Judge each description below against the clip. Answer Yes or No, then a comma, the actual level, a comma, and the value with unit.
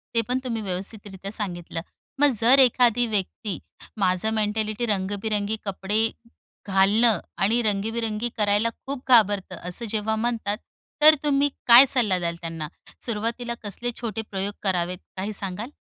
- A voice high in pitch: Yes, high, 215 Hz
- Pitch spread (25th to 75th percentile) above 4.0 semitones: No, average, 3.2 semitones